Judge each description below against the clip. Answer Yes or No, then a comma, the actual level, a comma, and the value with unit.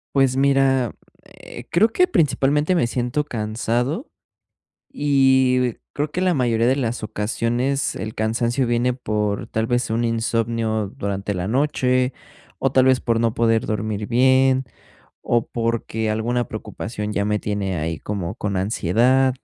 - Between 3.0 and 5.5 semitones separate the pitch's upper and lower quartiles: Yes, average, 3.3 semitones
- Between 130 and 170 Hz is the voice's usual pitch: No, low, 120 Hz